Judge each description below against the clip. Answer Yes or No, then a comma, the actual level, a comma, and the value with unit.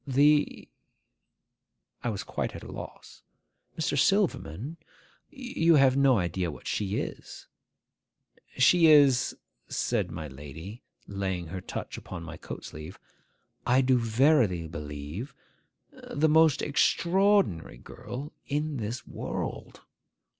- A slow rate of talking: Yes, slow, 115 wpm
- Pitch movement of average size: No, wide, 9.0 semitones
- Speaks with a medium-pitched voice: No, low, 125 Hz